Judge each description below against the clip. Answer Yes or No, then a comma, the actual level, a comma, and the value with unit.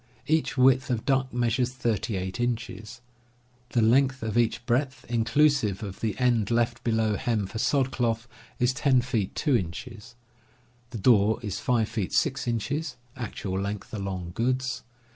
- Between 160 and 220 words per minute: No, average, 150 wpm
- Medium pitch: No, low, 120 Hz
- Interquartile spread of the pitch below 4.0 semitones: Yes, average, 2.9 semitones